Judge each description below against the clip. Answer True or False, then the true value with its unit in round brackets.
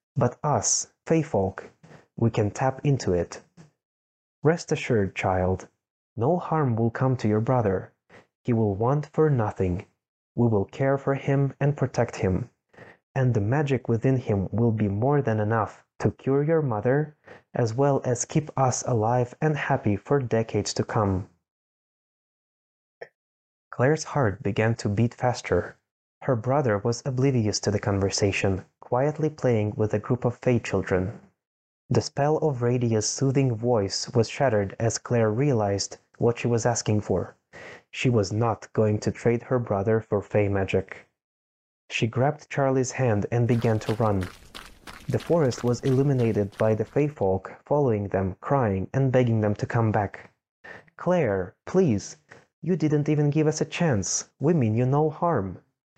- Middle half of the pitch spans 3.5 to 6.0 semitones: True (4.8 semitones)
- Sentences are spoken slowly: False (155 wpm)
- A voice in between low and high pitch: False (120 Hz)